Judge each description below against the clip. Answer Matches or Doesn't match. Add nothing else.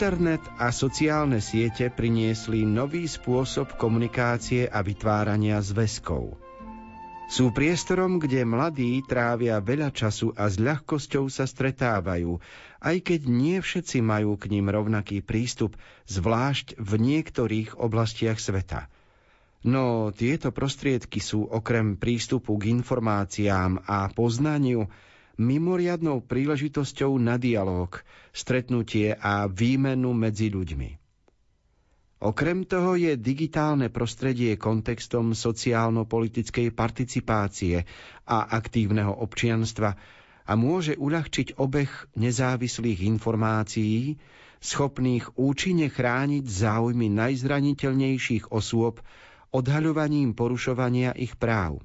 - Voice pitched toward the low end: Matches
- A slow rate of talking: Matches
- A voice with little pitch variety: Doesn't match